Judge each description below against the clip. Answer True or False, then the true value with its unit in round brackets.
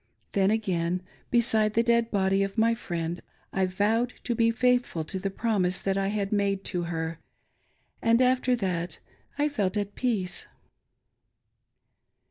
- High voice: True (200 Hz)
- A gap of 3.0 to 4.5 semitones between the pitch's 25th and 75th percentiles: True (3.8 semitones)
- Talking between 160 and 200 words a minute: False (145 wpm)